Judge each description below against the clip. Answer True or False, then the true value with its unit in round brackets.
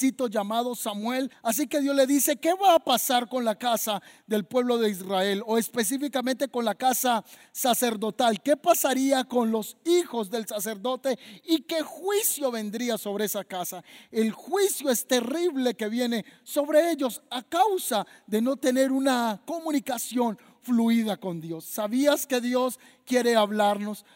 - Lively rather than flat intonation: False (3.7 semitones)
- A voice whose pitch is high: True (245 Hz)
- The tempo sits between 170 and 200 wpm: False (150 wpm)